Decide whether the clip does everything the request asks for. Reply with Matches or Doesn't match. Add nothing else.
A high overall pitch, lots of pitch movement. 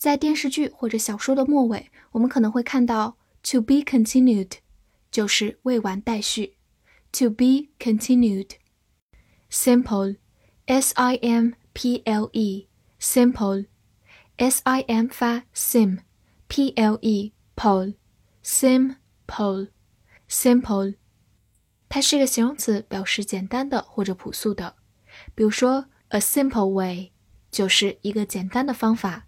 Doesn't match